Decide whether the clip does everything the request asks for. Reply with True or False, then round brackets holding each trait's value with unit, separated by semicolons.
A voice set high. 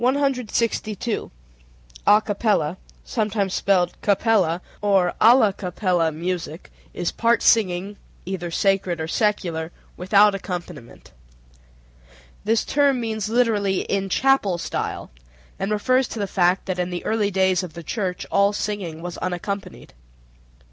True (195 Hz)